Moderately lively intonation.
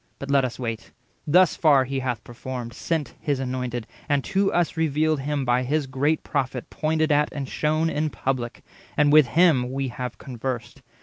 Yes: average, 3.4 semitones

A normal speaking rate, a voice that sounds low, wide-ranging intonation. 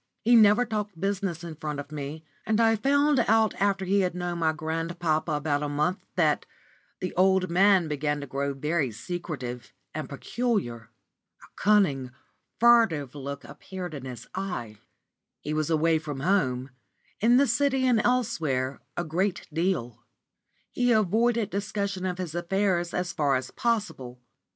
No: average, 150 wpm; medium, 175 Hz; wide, 5.8 semitones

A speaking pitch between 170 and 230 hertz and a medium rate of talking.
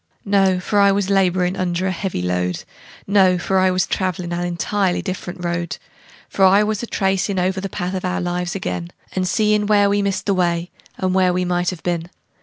No: medium, 185 Hz; fast, 210 wpm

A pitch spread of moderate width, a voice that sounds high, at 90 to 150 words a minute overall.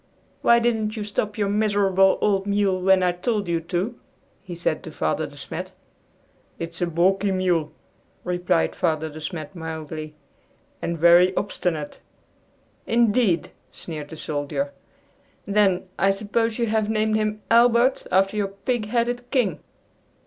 Yes: average, 4.0 semitones; high, 195 Hz; average, 140 wpm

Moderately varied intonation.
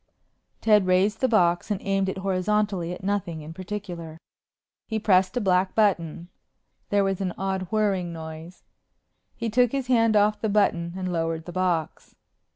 Yes: average, 3.2 semitones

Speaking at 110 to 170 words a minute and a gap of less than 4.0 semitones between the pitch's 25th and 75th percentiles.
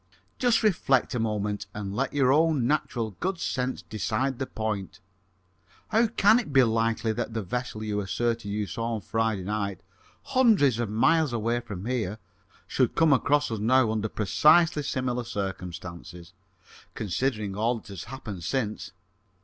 No: average, 155 wpm; average, 4.3 semitones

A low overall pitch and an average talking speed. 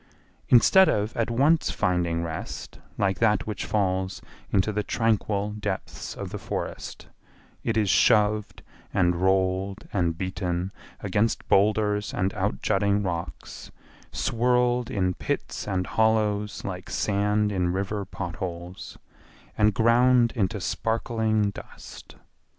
No: low, 105 Hz; slow, 120 wpm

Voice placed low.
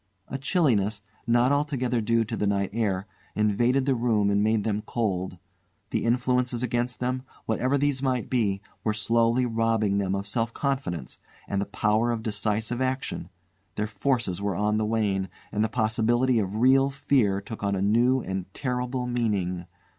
Yes: low, 115 Hz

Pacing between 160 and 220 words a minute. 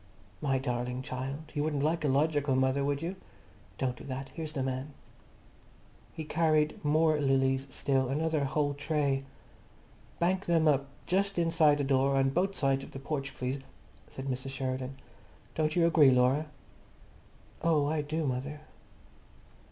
No: average, 150 wpm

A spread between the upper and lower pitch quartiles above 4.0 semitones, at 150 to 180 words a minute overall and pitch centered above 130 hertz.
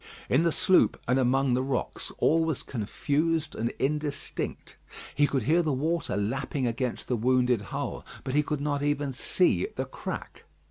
No: average, 3.1 semitones; average, 170 wpm; medium, 140 Hz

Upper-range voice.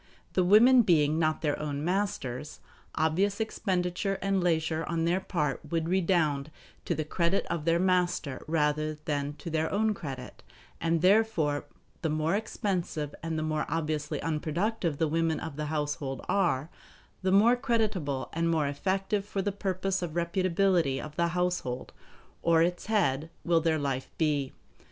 No: medium, 165 Hz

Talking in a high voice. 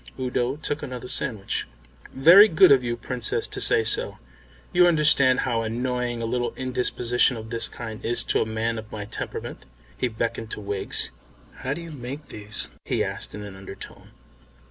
No: low, 120 Hz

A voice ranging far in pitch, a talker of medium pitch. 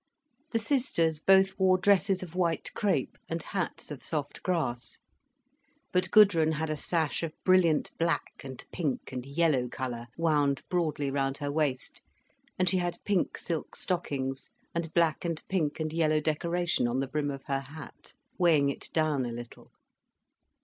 No: average, 4.0 semitones; medium, 160 Hz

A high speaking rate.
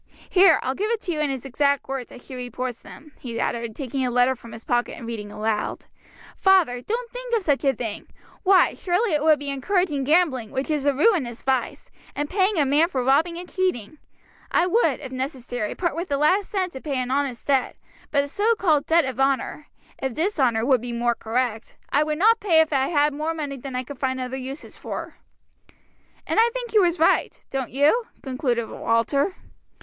Yes: fast, 210 wpm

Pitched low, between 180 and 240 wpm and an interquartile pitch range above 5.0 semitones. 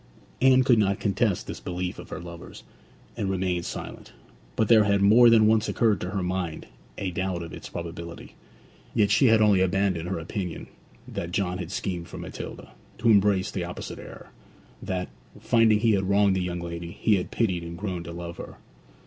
No: very low, 95 Hz; average, 190 wpm; average, 3.2 semitones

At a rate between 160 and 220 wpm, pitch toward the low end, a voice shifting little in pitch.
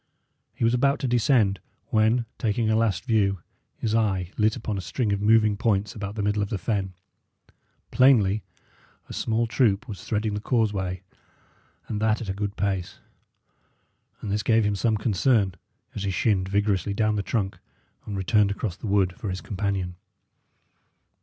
Yes: average, 170 wpm; low, 105 Hz; narrow, 2.2 semitones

